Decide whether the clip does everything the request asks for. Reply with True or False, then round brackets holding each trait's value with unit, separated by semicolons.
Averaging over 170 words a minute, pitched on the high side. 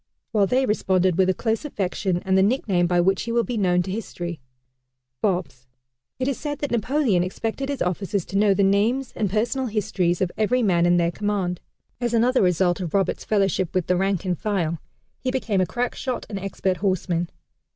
True (200 wpm; 195 Hz)